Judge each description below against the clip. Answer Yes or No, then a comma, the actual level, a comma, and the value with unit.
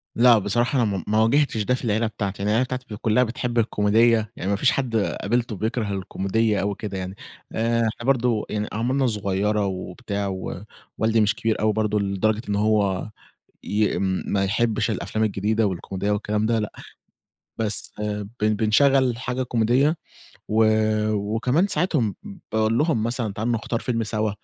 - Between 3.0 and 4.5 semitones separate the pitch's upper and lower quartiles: No, narrow, 2.4 semitones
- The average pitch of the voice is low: Yes, low, 110 Hz